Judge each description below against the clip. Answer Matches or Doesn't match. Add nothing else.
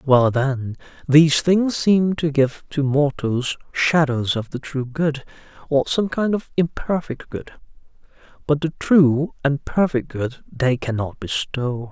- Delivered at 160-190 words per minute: Doesn't match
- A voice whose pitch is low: Doesn't match